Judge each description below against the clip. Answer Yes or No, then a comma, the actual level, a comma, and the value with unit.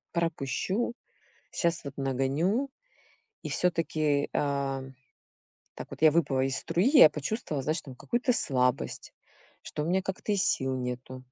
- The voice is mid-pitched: Yes, medium, 150 Hz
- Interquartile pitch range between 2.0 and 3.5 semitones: No, average, 4.7 semitones